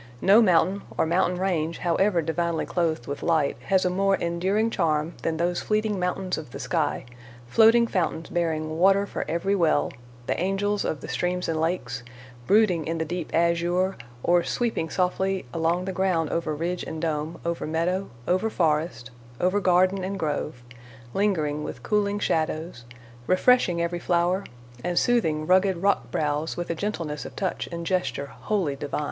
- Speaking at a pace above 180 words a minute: No, average, 165 wpm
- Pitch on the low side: No, medium, 175 Hz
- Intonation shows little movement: No, average, 3.1 semitones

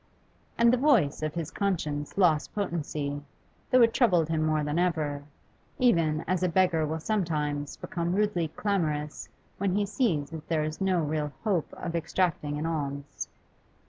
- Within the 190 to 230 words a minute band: No, average, 160 wpm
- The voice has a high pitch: No, medium, 165 Hz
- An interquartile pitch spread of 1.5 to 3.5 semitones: No, average, 3.9 semitones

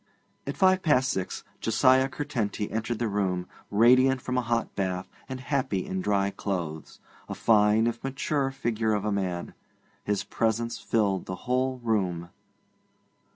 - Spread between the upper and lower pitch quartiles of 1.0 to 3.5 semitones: No, average, 4.5 semitones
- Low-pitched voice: Yes, low, 110 Hz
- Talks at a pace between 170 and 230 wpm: No, average, 150 wpm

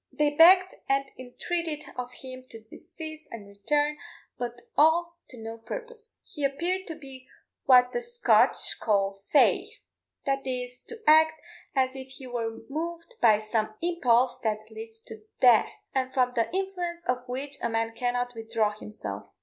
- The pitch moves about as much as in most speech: No, wide, 5.7 semitones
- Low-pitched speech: No, very high, 260 Hz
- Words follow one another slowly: No, average, 160 wpm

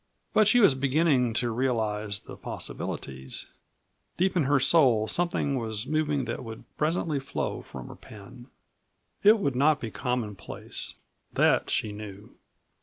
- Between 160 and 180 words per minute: No, average, 140 wpm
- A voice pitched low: Yes, low, 125 Hz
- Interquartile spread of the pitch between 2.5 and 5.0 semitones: No, wide, 5.5 semitones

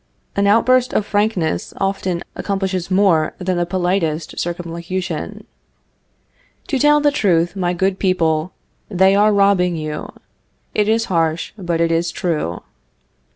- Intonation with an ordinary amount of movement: Yes, average, 3.0 semitones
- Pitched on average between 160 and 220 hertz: Yes, medium, 185 Hz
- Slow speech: Yes, slow, 130 wpm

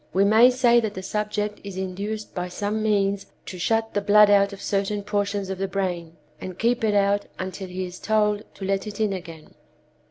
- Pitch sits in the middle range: No, high, 200 Hz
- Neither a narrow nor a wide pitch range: No, narrow, 1.9 semitones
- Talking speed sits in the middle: No, fast, 210 wpm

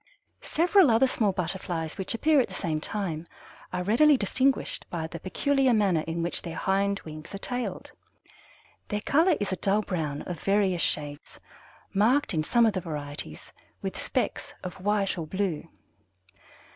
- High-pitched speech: Yes, high, 195 Hz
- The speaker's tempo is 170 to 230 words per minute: No, average, 160 wpm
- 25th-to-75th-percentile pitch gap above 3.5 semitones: Yes, wide, 5.4 semitones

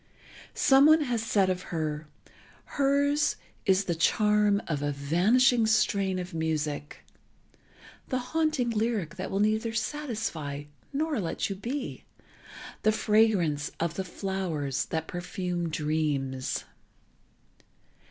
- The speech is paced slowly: Yes, slow, 110 wpm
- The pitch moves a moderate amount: No, wide, 6.4 semitones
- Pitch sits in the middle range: No, high, 195 Hz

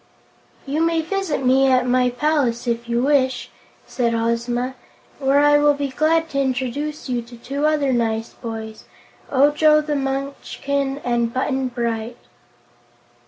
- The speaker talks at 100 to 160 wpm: Yes, average, 140 wpm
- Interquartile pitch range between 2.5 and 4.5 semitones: Yes, average, 3.4 semitones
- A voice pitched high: Yes, very high, 265 Hz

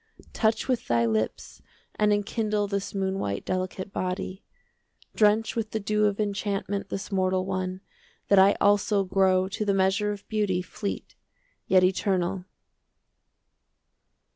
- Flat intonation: Yes, narrow, 1.9 semitones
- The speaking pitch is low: No, high, 195 Hz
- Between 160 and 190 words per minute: No, average, 140 wpm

